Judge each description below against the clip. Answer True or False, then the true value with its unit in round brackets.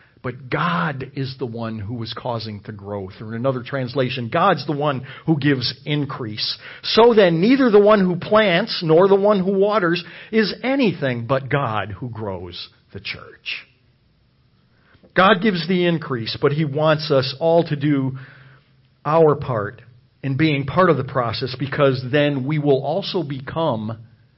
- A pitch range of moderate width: True (5.0 semitones)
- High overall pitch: False (140 Hz)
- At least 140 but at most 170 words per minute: True (160 wpm)